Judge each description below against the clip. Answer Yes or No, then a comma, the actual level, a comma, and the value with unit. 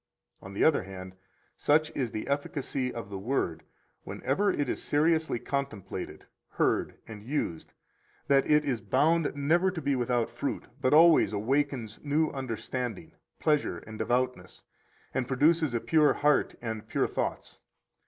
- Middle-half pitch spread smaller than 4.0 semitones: No, average, 5.1 semitones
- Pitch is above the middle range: No, low, 135 Hz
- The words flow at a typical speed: Yes, average, 150 wpm